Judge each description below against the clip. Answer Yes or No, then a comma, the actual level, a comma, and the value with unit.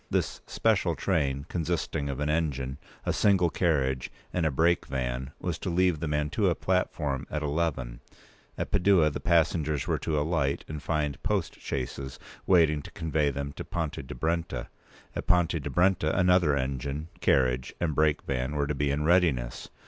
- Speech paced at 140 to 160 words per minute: No, average, 170 wpm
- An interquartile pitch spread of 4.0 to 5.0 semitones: No, average, 3.5 semitones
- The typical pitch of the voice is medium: No, very low, 75 Hz